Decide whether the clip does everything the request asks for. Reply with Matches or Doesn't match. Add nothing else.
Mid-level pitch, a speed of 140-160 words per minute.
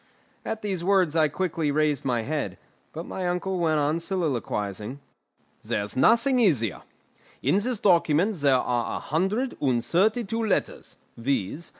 Matches